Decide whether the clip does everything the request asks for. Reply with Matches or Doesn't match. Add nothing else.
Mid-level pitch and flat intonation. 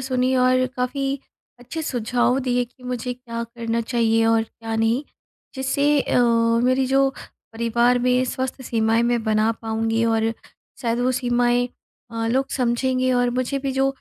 Doesn't match